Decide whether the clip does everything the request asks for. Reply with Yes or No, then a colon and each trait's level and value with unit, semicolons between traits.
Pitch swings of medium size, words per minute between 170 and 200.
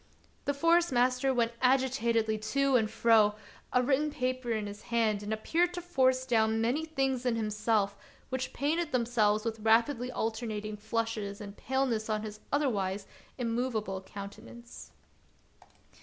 No: average, 3.3 semitones; average, 140 wpm